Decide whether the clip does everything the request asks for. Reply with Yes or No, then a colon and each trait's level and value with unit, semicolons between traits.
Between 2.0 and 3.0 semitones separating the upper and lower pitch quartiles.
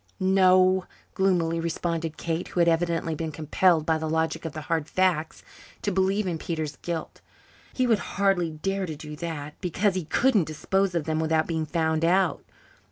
Yes: average, 2.7 semitones